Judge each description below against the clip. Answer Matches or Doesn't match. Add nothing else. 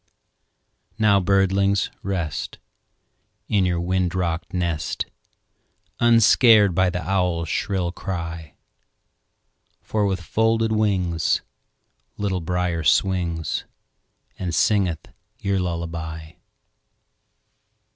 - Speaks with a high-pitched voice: Doesn't match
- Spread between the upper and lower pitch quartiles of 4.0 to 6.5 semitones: Doesn't match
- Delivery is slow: Matches